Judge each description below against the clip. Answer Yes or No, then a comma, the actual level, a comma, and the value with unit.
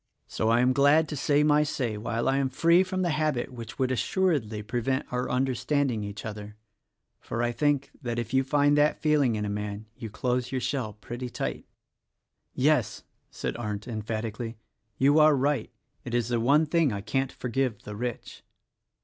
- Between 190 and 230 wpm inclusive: Yes, average, 200 wpm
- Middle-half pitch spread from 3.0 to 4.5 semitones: Yes, average, 4.2 semitones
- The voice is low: Yes, low, 125 Hz